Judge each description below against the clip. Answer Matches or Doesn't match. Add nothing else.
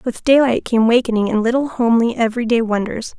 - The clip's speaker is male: Doesn't match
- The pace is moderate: Matches